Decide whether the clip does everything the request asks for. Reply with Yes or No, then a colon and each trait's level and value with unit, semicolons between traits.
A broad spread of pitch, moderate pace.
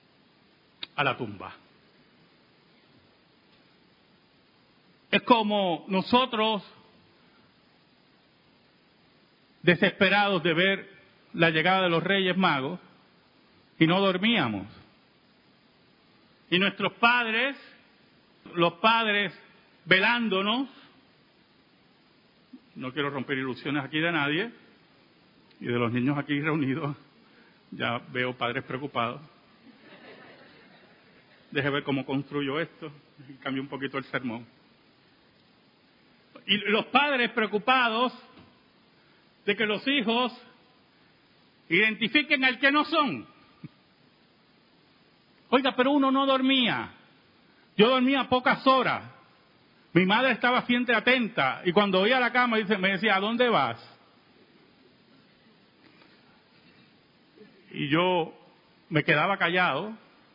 No: wide, 7.3 semitones; slow, 95 wpm